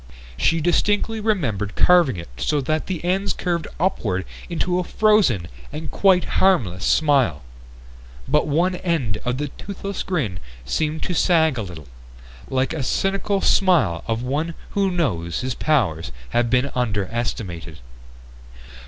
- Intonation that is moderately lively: No, wide, 8.5 semitones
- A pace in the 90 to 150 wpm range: Yes, slow, 135 wpm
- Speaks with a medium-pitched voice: Yes, medium, 150 Hz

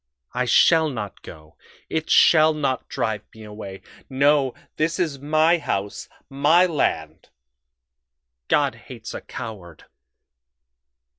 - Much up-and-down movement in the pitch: Yes, wide, 6.9 semitones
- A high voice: No, low, 135 Hz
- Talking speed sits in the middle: No, slow, 115 wpm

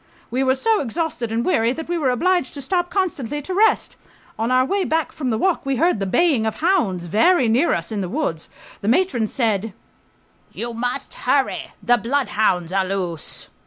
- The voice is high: Yes, very high, 255 Hz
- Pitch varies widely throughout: Yes, wide, 7.2 semitones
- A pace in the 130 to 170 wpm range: No, average, 195 wpm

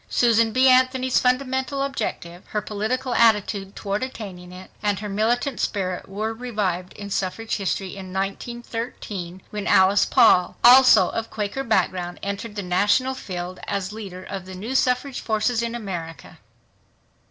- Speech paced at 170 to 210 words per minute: No, average, 145 wpm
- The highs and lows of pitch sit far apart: No, average, 4.3 semitones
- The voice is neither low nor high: No, high, 210 Hz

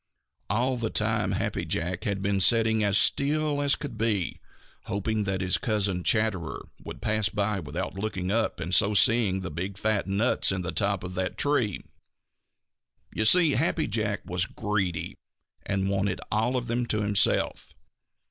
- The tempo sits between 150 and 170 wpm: Yes, average, 165 wpm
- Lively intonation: No, average, 2.9 semitones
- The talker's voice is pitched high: No, low, 105 Hz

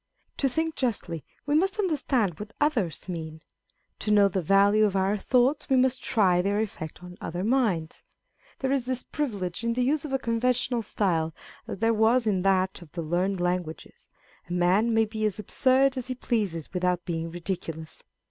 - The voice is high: Yes, high, 210 Hz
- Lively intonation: Yes, wide, 6.0 semitones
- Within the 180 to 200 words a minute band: Yes, average, 185 wpm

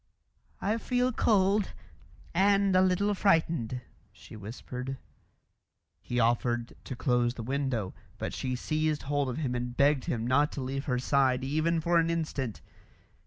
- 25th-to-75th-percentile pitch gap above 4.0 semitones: Yes, average, 5.2 semitones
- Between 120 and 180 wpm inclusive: Yes, average, 150 wpm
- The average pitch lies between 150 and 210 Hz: No, medium, 140 Hz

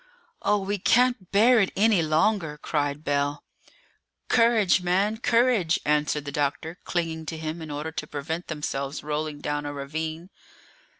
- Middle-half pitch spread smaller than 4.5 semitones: No, average, 5.0 semitones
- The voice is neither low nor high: Yes, medium, 160 Hz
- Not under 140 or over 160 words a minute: Yes, average, 145 wpm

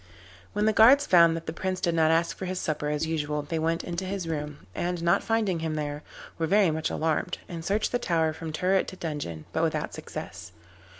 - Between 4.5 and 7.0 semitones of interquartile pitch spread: No, average, 3.0 semitones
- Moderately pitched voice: Yes, medium, 165 Hz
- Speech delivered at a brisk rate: Yes, fast, 220 wpm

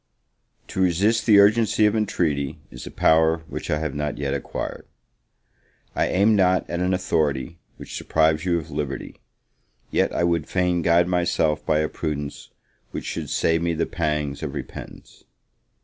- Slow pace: No, average, 165 wpm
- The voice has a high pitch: No, very low, 85 Hz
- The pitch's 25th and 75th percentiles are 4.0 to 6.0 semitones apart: No, average, 3.1 semitones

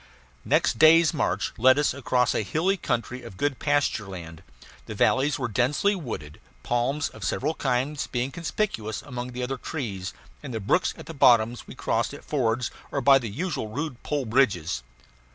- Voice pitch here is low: Yes, low, 130 Hz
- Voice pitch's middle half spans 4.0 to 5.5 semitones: Yes, average, 4.3 semitones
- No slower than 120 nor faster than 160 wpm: No, average, 170 wpm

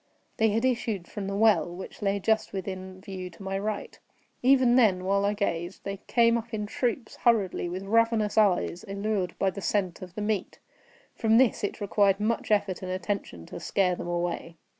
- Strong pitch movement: No, average, 2.9 semitones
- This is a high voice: Yes, high, 200 Hz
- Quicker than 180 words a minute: Yes, average, 190 wpm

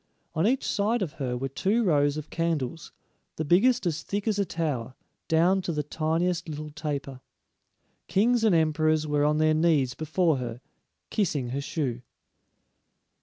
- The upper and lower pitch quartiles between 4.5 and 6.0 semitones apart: No, average, 3.8 semitones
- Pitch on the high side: No, medium, 155 Hz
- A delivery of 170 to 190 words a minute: No, average, 160 wpm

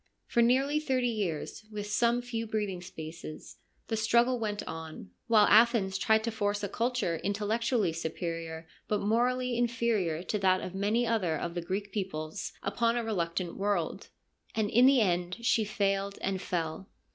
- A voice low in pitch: No, high, 205 Hz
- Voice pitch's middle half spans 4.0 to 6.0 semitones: Yes, average, 4.5 semitones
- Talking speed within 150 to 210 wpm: Yes, average, 160 wpm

